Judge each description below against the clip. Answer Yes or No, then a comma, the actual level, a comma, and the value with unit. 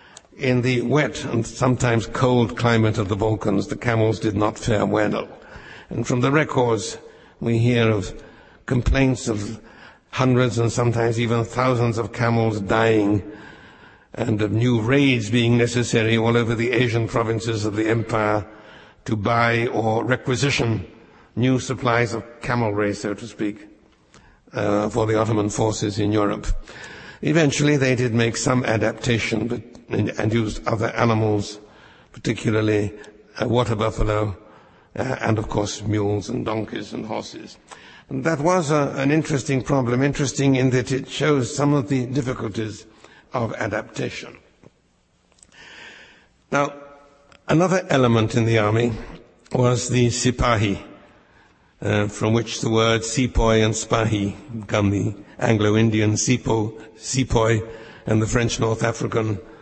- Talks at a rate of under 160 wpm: Yes, slow, 135 wpm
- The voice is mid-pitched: No, low, 115 Hz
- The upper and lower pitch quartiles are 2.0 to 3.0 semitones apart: Yes, narrow, 2.5 semitones